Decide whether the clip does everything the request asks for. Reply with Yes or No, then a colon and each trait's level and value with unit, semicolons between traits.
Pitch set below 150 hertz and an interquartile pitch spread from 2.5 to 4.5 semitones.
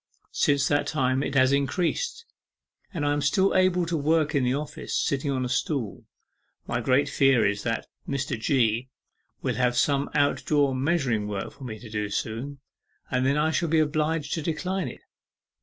Yes: medium, 140 Hz; average, 3.4 semitones